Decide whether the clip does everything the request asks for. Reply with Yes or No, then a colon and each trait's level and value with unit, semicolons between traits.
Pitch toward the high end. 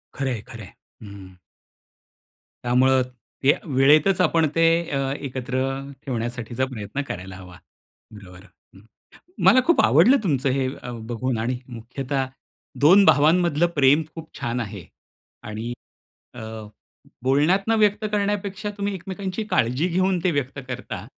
No: low, 135 Hz